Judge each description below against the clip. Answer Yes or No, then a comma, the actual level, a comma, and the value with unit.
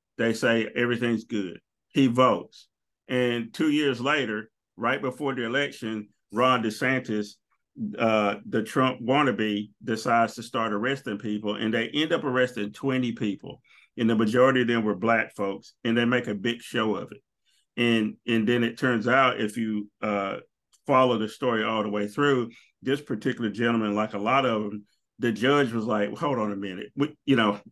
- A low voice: Yes, low, 115 Hz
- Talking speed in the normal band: Yes, average, 180 wpm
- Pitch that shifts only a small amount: No, average, 3.2 semitones